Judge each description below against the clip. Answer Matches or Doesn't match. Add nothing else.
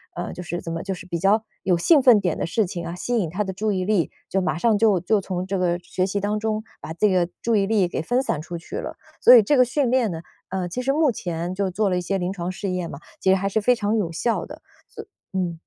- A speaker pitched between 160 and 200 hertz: Matches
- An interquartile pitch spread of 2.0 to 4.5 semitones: Matches